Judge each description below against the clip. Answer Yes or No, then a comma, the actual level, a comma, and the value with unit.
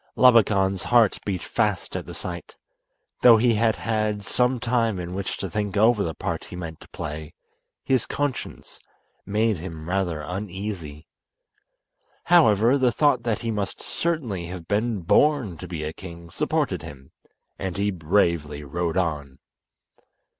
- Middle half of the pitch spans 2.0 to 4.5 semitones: No, average, 5.2 semitones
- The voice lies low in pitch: Yes, low, 100 Hz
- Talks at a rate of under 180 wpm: Yes, average, 150 wpm